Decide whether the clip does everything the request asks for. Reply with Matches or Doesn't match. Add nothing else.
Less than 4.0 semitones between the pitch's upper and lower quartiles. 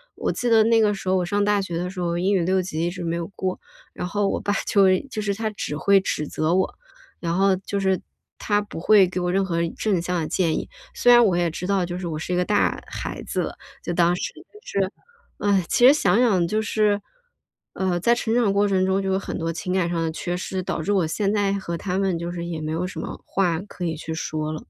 Matches